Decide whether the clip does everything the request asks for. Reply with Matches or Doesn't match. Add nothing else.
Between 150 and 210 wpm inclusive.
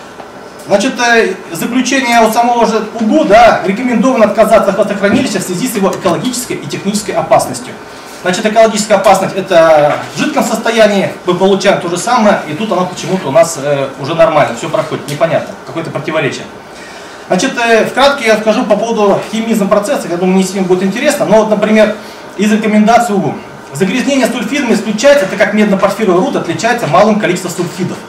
Matches